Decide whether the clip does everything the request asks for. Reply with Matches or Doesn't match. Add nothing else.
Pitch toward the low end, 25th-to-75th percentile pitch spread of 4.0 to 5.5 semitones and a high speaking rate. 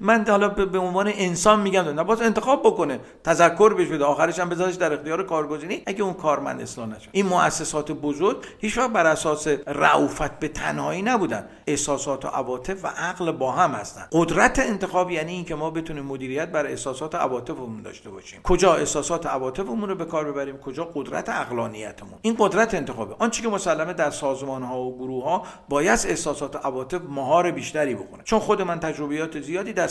Doesn't match